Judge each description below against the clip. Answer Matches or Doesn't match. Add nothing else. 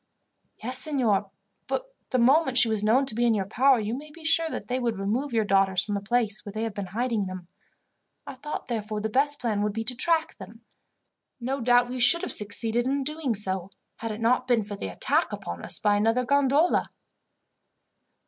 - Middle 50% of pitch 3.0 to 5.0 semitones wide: Matches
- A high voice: Matches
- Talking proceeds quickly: Matches